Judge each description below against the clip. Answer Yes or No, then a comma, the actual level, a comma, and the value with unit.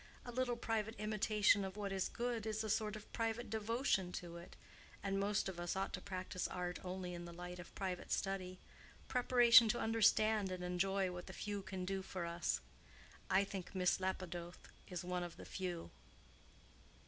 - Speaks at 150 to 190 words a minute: Yes, average, 180 wpm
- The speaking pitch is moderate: No, high, 195 Hz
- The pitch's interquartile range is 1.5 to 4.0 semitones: Yes, average, 3.2 semitones